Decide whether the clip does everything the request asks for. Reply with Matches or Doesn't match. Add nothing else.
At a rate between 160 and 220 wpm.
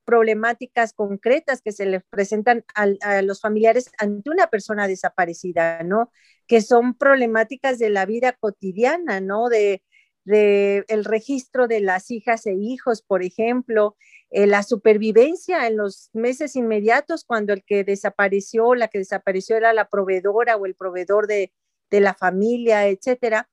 Doesn't match